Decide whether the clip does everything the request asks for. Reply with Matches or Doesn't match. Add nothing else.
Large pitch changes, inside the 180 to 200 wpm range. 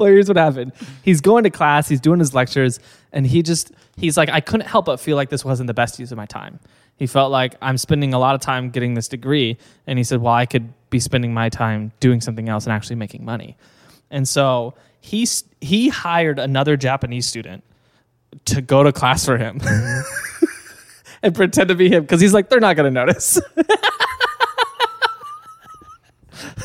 Matches